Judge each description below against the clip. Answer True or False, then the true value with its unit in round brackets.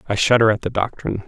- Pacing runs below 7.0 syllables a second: False (7.3 syllables/s)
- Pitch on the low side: True (110 Hz)